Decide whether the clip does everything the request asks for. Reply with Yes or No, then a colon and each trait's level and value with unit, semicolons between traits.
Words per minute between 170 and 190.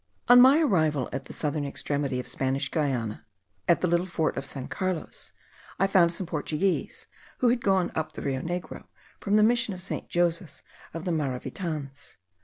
Yes: average, 180 wpm